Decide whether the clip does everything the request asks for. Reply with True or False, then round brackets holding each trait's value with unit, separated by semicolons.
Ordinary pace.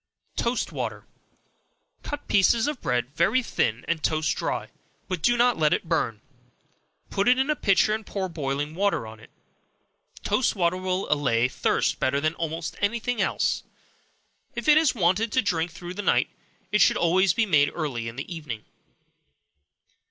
True (170 wpm)